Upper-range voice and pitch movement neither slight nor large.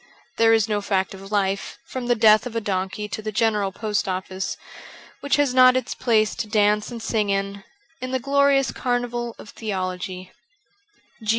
Yes: high, 215 Hz; average, 3.5 semitones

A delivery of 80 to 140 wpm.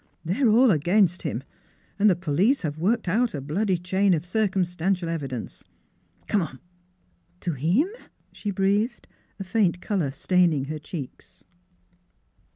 No: average, 155 wpm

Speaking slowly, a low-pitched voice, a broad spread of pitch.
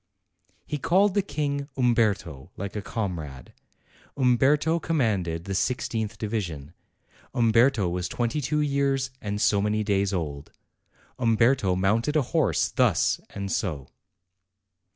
Yes: slow, 120 wpm; low, 110 Hz; wide, 6.3 semitones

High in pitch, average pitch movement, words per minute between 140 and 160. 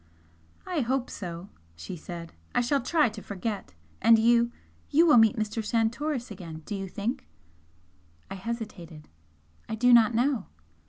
Yes: high, 225 Hz; average, 4.0 semitones; average, 150 wpm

